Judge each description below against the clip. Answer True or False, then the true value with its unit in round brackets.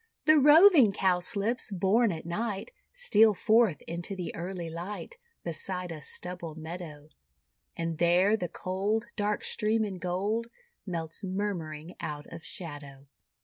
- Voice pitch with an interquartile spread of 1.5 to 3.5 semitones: False (4.3 semitones)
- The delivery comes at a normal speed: False (130 wpm)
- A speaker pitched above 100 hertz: True (185 Hz)